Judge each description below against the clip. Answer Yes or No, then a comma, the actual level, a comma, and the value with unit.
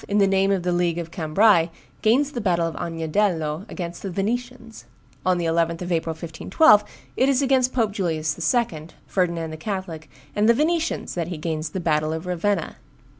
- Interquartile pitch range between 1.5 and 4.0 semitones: No, average, 4.5 semitones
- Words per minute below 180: No, average, 185 wpm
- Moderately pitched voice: Yes, medium, 180 Hz